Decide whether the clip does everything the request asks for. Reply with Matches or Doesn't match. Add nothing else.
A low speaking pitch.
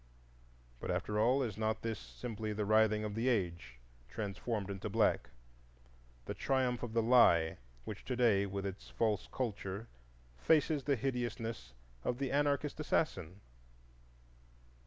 Matches